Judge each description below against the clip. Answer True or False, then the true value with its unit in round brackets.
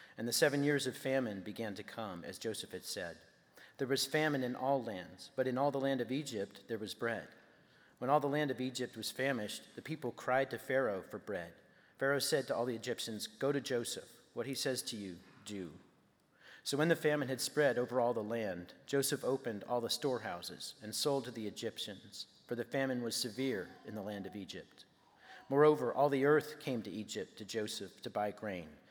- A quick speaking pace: True (210 wpm)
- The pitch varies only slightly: False (4.2 semitones)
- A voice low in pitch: True (125 Hz)